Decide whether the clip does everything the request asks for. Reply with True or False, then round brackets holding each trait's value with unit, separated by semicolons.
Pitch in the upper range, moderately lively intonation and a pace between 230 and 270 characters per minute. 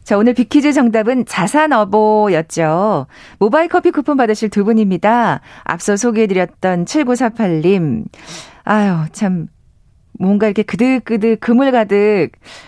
True (215 Hz; 3.6 semitones; 260 characters per minute)